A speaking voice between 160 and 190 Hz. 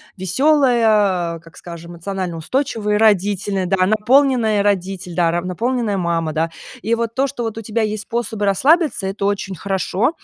No: high, 205 Hz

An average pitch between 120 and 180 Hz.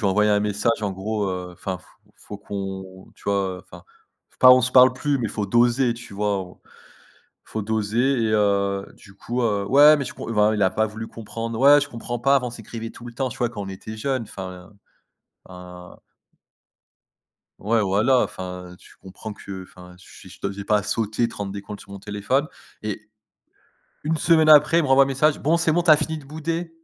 No: low, 110 Hz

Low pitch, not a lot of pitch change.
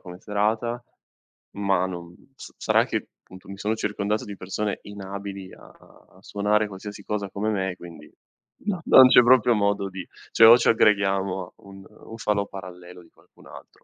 Yes: low, 100 Hz; narrow, 1.9 semitones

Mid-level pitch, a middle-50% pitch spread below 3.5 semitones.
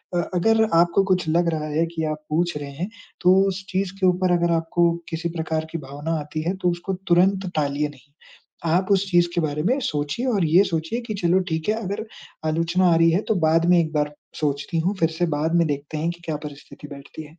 Yes: medium, 165 Hz; average, 2.8 semitones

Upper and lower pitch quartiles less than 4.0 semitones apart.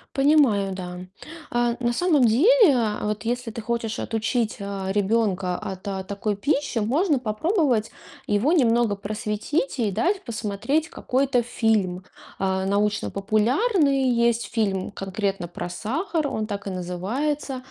No: average, 4.8 semitones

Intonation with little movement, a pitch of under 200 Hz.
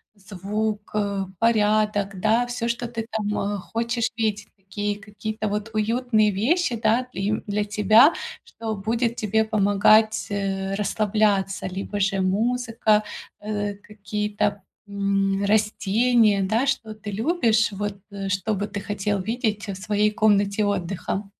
No: narrow, 1.7 semitones; high, 210 Hz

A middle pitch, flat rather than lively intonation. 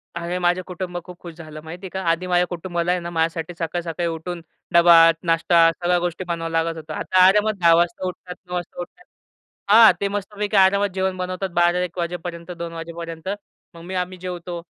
Yes: medium, 175 Hz; narrow, 1.5 semitones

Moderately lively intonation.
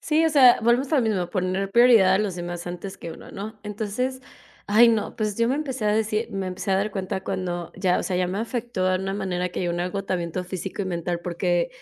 Yes: average, 3.5 semitones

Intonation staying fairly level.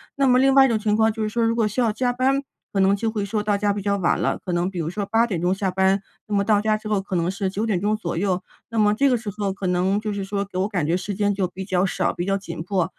Yes: narrow, 2.3 semitones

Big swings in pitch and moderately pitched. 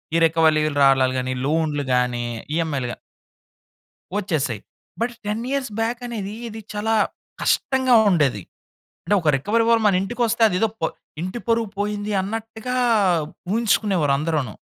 No: wide, 6.9 semitones; high, 195 Hz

